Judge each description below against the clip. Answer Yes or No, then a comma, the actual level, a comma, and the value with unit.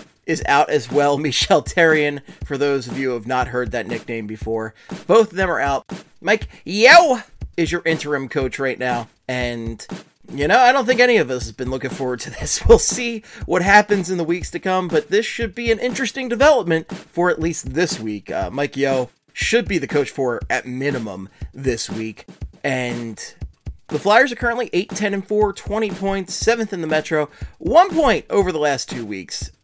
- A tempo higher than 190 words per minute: Yes, average, 200 wpm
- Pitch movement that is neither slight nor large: No, wide, 8.2 semitones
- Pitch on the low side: No, medium, 155 Hz